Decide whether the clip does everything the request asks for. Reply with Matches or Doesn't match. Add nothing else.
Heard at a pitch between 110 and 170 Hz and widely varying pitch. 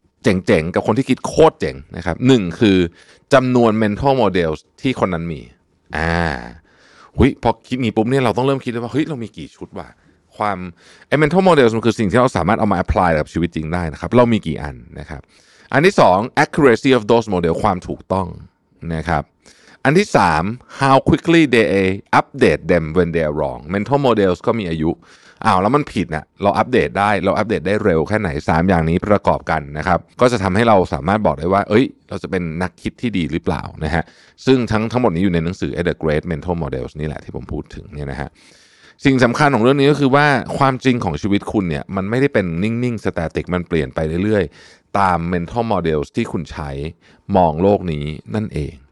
Doesn't match